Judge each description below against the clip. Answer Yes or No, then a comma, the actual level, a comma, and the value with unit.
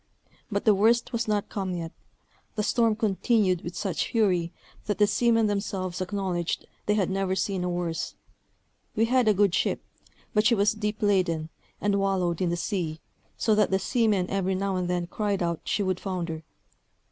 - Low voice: No, high, 195 Hz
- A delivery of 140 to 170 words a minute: No, average, 180 wpm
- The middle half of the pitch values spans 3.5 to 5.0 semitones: No, average, 2.9 semitones